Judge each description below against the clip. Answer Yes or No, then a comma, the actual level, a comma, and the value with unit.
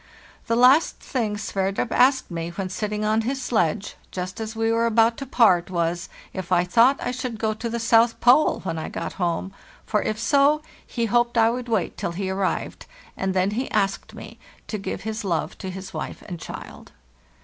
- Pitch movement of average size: Yes, average, 3.8 semitones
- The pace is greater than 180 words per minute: Yes, average, 200 wpm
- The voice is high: Yes, high, 215 Hz